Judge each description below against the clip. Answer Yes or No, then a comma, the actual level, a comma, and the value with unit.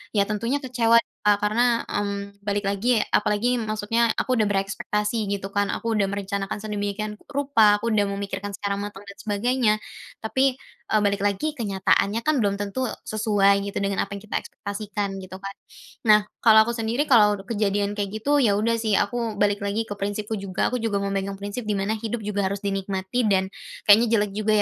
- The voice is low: No, high, 205 Hz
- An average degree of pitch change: No, narrow, 2.1 semitones